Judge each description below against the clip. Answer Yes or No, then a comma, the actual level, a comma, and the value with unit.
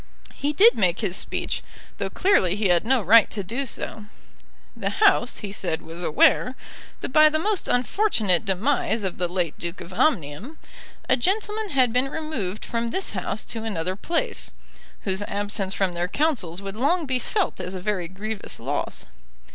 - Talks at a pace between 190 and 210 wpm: No, average, 175 wpm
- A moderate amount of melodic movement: No, wide, 7.6 semitones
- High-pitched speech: Yes, high, 215 Hz